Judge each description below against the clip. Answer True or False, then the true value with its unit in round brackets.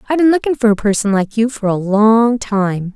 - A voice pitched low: False (220 Hz)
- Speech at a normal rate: False (245 wpm)